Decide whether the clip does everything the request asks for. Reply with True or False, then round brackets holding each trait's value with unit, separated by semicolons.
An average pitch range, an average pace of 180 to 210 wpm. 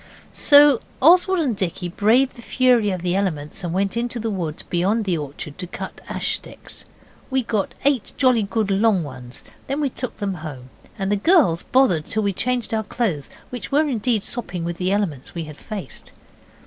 False (6.0 semitones; 190 wpm)